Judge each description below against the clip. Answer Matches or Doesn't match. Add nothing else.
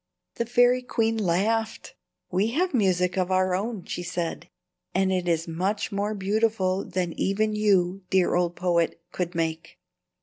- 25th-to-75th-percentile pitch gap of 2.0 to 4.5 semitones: Matches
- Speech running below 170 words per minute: Matches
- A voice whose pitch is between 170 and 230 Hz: Matches